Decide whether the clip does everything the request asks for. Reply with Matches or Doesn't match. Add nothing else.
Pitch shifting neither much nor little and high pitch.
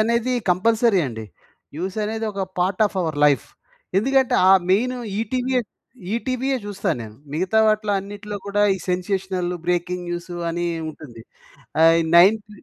Matches